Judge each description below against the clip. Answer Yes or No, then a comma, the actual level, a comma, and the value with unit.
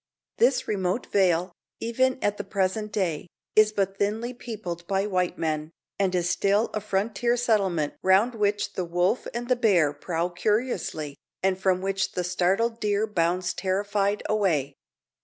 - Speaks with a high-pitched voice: Yes, high, 195 Hz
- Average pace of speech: Yes, average, 155 wpm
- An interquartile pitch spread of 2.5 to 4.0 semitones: Yes, average, 3.1 semitones